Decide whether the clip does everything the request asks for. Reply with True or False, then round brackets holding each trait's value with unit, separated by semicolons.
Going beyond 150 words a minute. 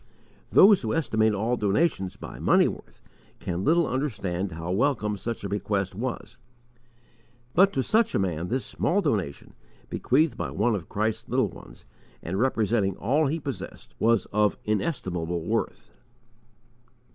False (145 wpm)